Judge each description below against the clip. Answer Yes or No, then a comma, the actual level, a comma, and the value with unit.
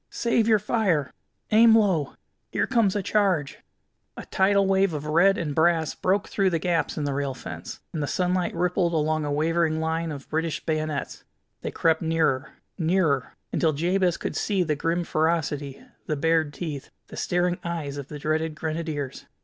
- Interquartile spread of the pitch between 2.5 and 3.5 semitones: Yes, average, 3.2 semitones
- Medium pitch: Yes, medium, 165 Hz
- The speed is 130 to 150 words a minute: No, average, 175 wpm